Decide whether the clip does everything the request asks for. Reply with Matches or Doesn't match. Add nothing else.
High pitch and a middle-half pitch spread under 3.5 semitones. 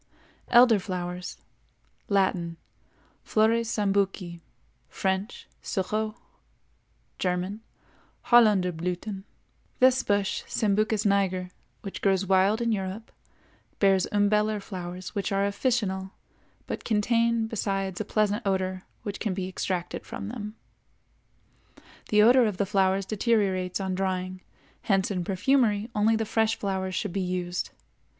Matches